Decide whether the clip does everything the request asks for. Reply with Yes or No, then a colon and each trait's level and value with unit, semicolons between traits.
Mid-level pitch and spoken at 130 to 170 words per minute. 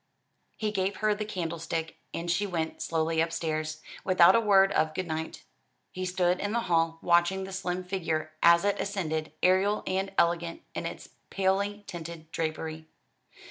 Yes: medium, 175 Hz; average, 160 wpm